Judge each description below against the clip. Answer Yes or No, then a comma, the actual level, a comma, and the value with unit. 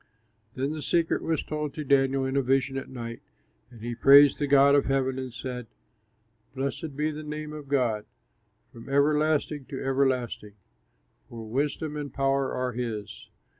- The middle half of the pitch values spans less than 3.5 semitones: Yes, narrow, 2.5 semitones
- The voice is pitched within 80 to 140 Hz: Yes, low, 135 Hz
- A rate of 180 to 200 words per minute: No, average, 165 wpm